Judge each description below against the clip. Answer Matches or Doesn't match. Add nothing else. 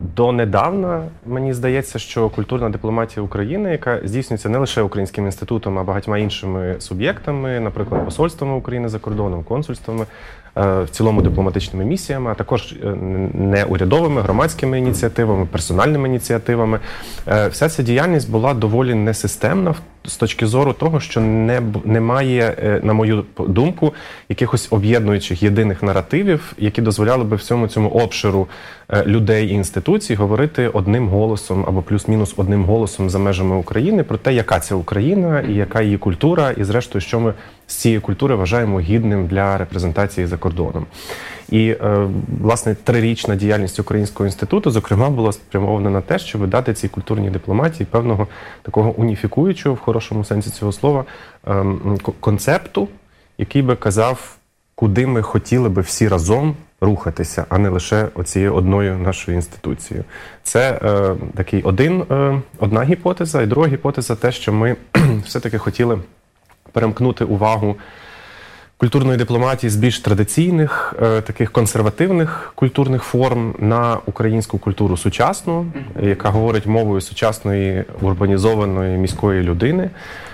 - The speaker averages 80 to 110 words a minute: Doesn't match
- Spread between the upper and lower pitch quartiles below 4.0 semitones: Matches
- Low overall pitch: Matches